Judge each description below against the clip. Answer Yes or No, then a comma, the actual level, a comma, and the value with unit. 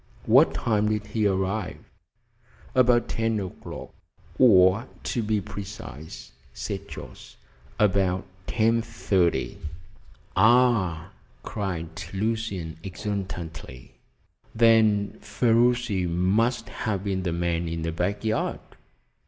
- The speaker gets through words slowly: Yes, slow, 100 wpm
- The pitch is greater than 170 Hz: No, low, 100 Hz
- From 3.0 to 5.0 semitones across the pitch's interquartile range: Yes, average, 3.8 semitones